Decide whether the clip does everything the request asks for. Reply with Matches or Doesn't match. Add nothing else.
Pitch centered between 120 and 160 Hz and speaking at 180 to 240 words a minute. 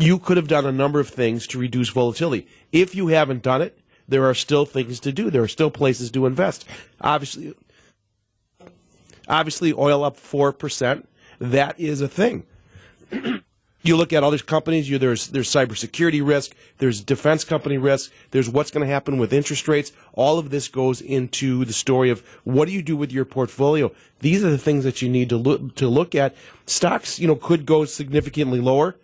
Matches